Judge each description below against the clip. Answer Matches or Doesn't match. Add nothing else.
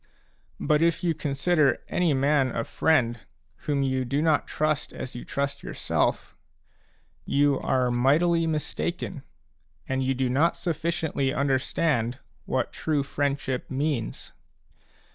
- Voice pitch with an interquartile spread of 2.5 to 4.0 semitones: Matches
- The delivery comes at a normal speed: Doesn't match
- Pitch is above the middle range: Doesn't match